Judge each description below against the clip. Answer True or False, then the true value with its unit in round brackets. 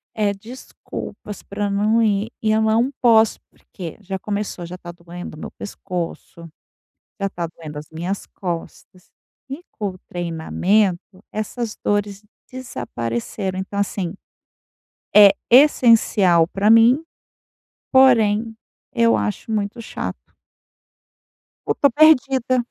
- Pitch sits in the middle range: False (205 Hz)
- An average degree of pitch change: True (4.0 semitones)